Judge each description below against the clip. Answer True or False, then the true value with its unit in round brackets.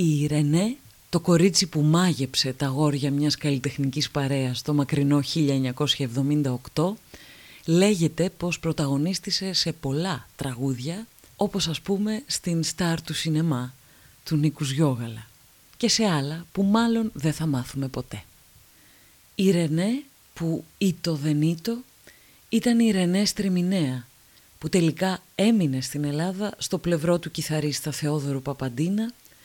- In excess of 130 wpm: False (120 wpm)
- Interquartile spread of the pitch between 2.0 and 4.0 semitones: False (4.7 semitones)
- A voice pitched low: False (155 Hz)